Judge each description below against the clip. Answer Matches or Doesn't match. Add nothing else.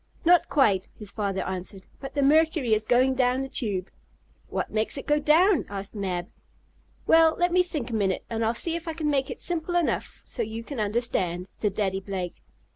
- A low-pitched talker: Doesn't match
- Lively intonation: Matches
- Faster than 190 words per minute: Matches